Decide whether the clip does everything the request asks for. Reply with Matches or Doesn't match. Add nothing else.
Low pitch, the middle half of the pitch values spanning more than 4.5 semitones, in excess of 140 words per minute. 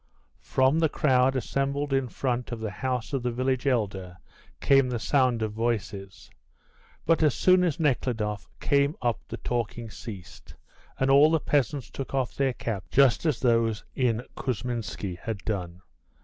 Doesn't match